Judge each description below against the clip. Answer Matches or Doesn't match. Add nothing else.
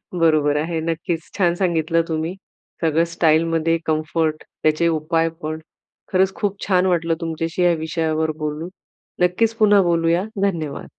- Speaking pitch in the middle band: Matches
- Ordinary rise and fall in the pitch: Doesn't match